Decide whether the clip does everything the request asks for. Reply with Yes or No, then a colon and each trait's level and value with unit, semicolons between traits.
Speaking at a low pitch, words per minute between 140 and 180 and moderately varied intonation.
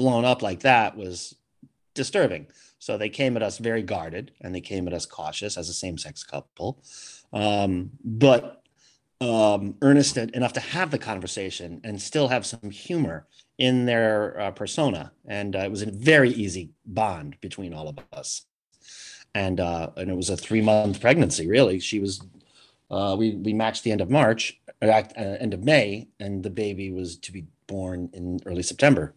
Yes: low, 105 Hz; average, 175 wpm; average, 3.6 semitones